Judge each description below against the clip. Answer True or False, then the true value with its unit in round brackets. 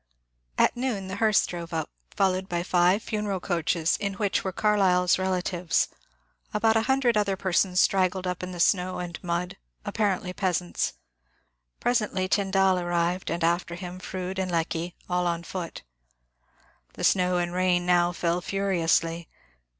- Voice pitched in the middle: True (180 Hz)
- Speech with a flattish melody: True (1.8 semitones)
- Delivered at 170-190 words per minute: False (150 wpm)